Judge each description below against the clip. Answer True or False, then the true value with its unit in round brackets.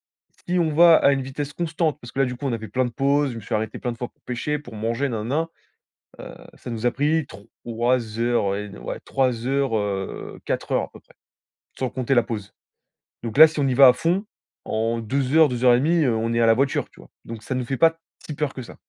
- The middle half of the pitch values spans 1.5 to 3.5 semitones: False (3.9 semitones)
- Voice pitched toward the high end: False (125 Hz)